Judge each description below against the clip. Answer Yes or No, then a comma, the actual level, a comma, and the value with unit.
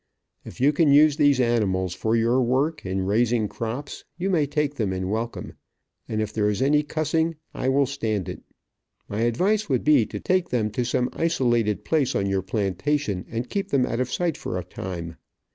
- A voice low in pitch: Yes, low, 120 Hz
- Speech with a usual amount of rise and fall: No, wide, 5.7 semitones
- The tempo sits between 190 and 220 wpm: Yes, average, 195 wpm